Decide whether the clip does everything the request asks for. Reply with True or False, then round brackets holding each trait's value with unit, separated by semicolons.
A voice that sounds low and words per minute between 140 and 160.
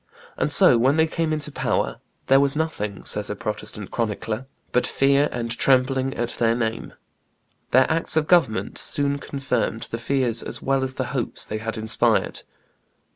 False (130 Hz; 170 wpm)